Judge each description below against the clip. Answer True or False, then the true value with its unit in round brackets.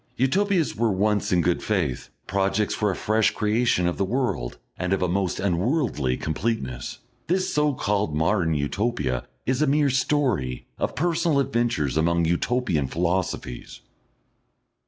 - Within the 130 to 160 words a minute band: True (140 wpm)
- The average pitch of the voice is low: True (100 Hz)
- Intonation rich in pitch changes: True (7.1 semitones)